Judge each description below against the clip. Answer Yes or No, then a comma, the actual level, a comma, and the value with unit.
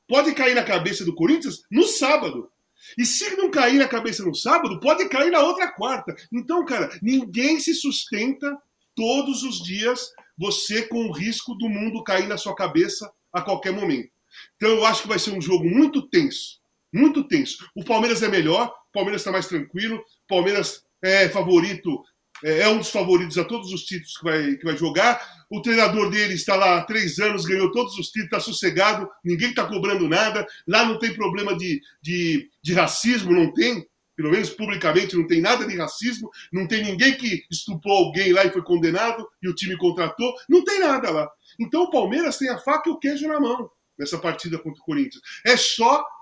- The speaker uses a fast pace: Yes, fast, 195 wpm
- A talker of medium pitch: No, high, 220 Hz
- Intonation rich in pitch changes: Yes, wide, 6.0 semitones